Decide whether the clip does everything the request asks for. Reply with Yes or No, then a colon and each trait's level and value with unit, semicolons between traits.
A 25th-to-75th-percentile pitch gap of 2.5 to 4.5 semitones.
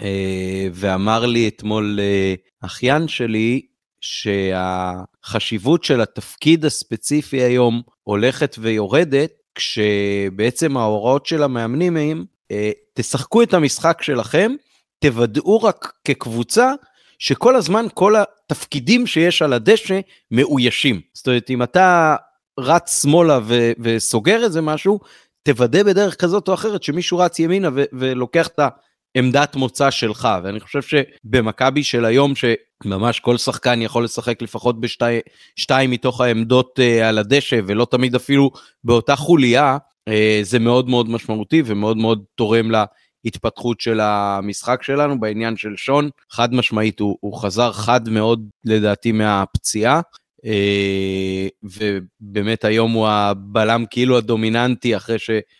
No: average, 5.1 semitones